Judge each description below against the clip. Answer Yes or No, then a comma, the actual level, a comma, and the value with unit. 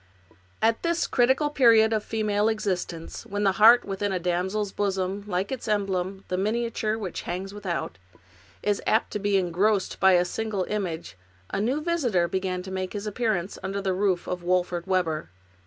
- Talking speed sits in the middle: Yes, average, 170 wpm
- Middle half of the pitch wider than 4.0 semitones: No, average, 3.0 semitones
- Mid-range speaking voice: No, high, 200 Hz